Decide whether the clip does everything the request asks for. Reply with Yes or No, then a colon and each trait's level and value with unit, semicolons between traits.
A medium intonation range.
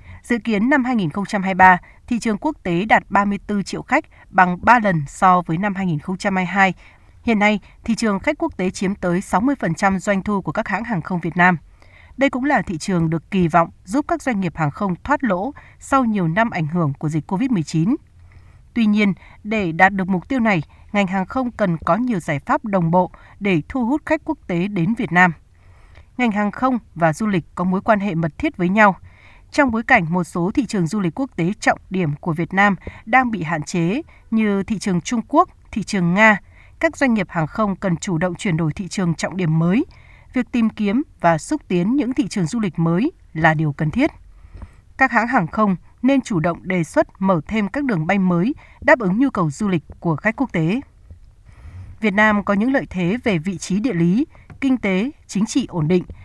Yes: average, 5.0 semitones